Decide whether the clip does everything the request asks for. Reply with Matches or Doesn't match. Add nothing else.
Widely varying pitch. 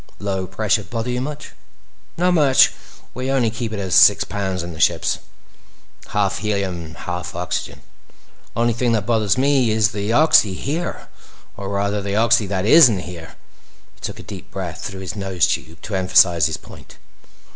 Doesn't match